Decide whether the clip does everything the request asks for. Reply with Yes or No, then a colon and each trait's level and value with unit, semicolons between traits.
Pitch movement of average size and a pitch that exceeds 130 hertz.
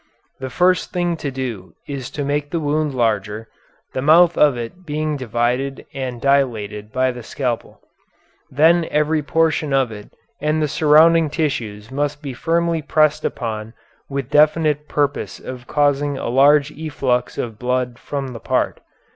Yes: average, 3.7 semitones; medium, 140 Hz